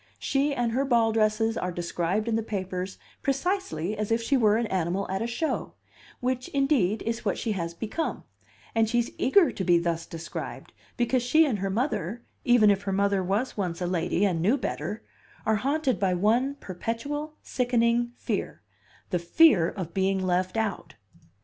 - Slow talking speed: No, average, 175 wpm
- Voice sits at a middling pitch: No, high, 215 Hz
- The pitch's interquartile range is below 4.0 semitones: No, average, 4.7 semitones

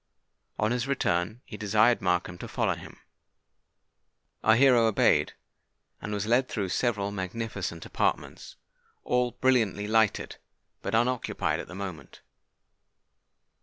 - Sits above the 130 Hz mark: No, low, 110 Hz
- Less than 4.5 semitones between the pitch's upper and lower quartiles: Yes, average, 3.6 semitones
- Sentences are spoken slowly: Yes, slow, 120 wpm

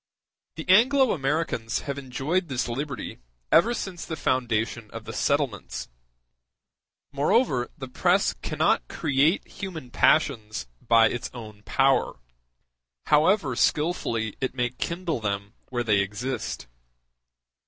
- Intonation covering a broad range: Yes, wide, 5.7 semitones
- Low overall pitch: Yes, low, 130 Hz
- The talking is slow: Yes, slow, 115 wpm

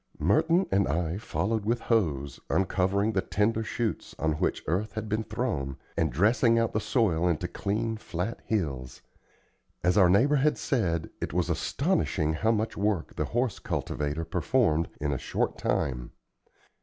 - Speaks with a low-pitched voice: Yes, low, 100 Hz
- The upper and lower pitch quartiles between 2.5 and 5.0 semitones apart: No, wide, 5.6 semitones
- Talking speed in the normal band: Yes, average, 155 wpm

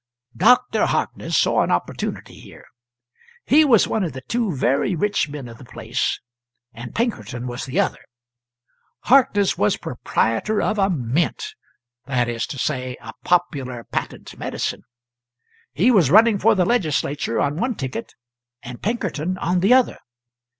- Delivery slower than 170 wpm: Yes, average, 150 wpm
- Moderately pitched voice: Yes, medium, 170 Hz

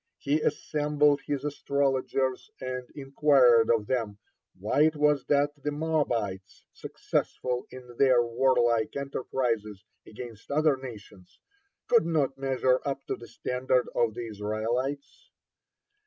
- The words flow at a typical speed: No, slow, 120 wpm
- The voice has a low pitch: Yes, low, 130 Hz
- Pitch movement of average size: Yes, average, 3.3 semitones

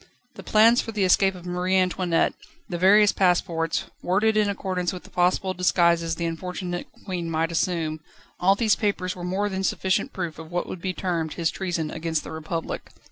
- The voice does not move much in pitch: Yes, narrow, 2.2 semitones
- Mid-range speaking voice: Yes, medium, 180 Hz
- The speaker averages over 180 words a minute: Yes, average, 190 wpm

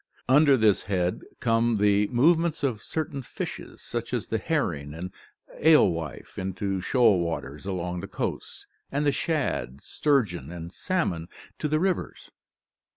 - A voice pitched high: No, low, 110 Hz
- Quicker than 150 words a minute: No, average, 145 wpm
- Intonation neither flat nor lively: No, wide, 8.4 semitones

